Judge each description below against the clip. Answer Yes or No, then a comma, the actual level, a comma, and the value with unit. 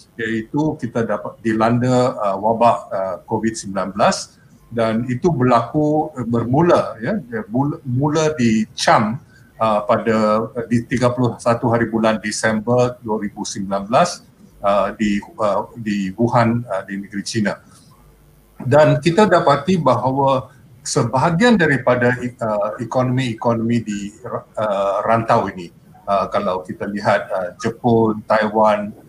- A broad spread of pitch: No, average, 2.8 semitones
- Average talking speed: No, slow, 85 wpm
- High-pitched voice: No, low, 120 Hz